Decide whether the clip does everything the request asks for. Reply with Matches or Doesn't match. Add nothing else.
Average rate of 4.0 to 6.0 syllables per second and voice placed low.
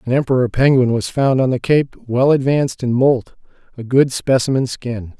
Matches